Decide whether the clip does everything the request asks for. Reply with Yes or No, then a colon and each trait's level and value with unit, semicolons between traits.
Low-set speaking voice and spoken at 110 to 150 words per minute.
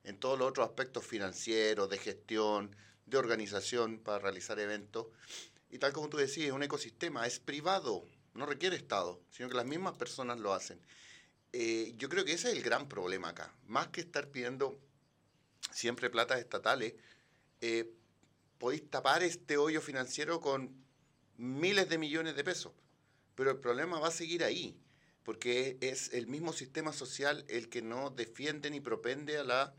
No: low, 130 Hz; average, 165 wpm